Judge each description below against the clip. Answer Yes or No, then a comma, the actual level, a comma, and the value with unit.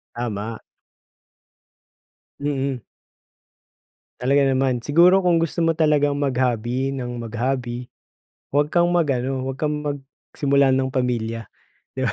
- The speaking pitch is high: No, low, 135 Hz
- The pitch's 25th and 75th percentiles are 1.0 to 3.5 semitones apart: Yes, average, 3.0 semitones